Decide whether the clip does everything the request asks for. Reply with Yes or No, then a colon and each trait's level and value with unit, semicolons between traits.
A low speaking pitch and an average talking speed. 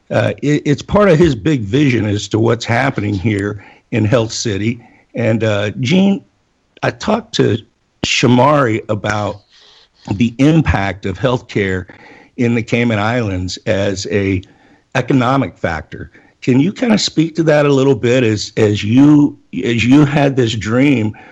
Yes: low, 120 Hz; average, 150 wpm